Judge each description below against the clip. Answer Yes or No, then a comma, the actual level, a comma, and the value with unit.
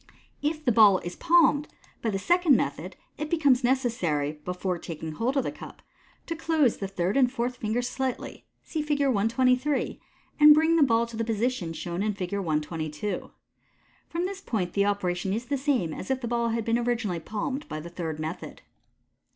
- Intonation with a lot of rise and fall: Yes, wide, 7.0 semitones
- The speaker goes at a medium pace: Yes, average, 190 wpm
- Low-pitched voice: No, high, 230 Hz